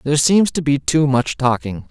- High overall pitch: No, medium, 140 Hz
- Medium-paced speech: No, fast, 220 wpm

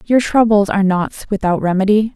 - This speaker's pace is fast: No, average, 165 wpm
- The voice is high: Yes, high, 205 Hz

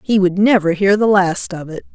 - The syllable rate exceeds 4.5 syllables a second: Yes, 5.0 syllables/s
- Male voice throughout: No, female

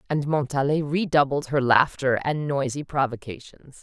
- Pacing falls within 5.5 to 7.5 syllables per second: No, 4.7 syllables/s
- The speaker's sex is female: Yes, female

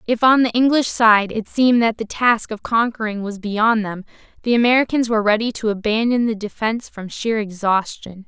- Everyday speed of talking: Yes, average, 190 wpm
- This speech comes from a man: No, female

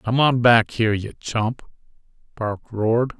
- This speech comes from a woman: No, male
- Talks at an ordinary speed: Yes, average, 150 wpm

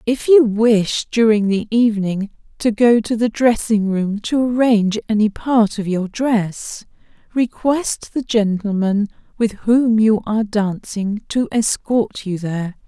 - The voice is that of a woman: Yes, female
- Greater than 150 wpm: No, average, 145 wpm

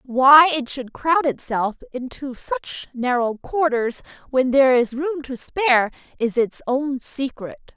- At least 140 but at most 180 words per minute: Yes, average, 145 wpm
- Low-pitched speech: No, very high, 265 Hz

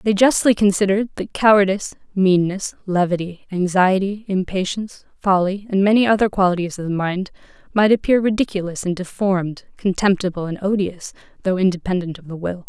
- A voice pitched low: No, high, 190 Hz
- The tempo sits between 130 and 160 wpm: Yes, average, 140 wpm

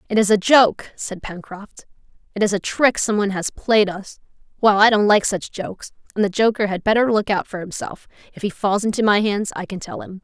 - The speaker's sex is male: No, female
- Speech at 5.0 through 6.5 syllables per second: Yes, 5.4 syllables/s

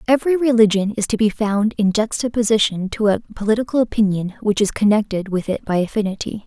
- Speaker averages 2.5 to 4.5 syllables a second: No, 6.2 syllables/s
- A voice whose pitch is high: Yes, high, 215 Hz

